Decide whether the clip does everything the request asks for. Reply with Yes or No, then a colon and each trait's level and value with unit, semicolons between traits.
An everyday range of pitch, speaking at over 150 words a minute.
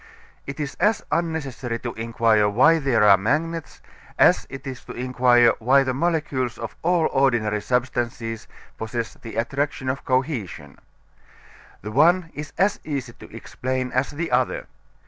No: average, 4.0 semitones; average, 145 wpm